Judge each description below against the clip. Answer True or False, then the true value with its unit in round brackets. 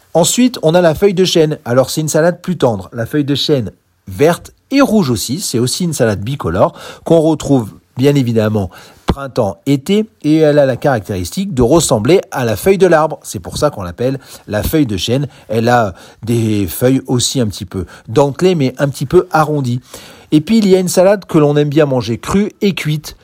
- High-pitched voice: False (140 Hz)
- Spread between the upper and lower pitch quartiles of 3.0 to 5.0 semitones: False (5.5 semitones)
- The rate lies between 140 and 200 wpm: False (210 wpm)